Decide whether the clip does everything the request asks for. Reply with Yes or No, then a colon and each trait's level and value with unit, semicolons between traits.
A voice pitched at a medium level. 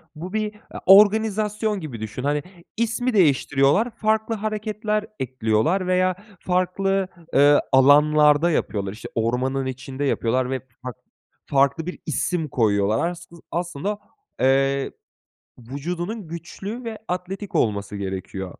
Yes: medium, 160 Hz